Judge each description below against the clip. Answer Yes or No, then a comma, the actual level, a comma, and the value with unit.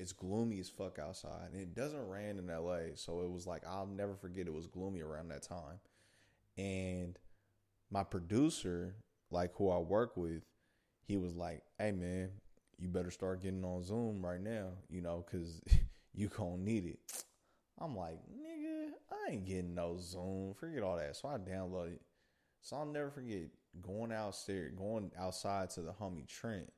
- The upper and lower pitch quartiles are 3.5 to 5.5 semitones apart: No, narrow, 2.6 semitones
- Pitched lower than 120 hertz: Yes, very low, 95 Hz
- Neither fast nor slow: Yes, average, 175 wpm